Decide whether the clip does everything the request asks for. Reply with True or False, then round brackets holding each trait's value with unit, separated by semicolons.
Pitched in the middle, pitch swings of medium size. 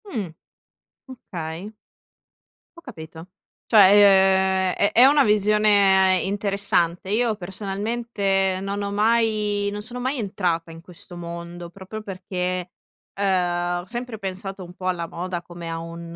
False (195 Hz; 3.0 semitones)